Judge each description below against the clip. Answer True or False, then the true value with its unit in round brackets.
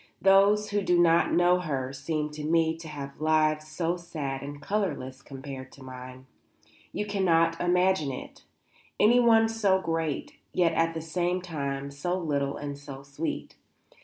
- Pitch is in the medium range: True (160 Hz)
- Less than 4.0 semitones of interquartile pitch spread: False (4.3 semitones)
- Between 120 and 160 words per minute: True (155 wpm)